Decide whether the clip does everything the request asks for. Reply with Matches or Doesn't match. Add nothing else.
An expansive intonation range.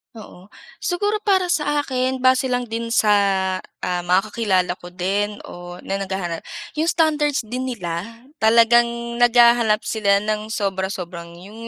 Doesn't match